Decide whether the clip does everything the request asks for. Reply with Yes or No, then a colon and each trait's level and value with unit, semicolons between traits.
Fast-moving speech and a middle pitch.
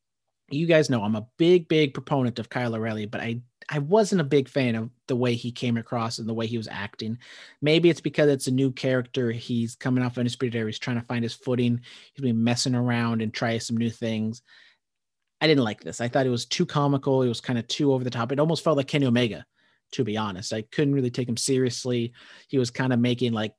No: fast, 245 wpm; low, 125 Hz